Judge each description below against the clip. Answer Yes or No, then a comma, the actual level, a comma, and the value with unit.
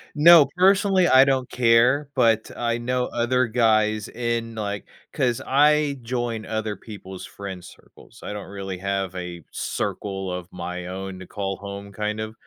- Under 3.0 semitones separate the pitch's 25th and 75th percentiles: No, average, 4.4 semitones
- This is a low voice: Yes, low, 110 Hz